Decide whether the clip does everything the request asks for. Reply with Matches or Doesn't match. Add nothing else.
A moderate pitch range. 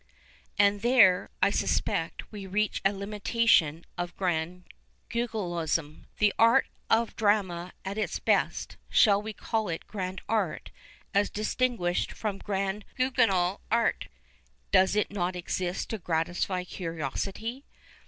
Matches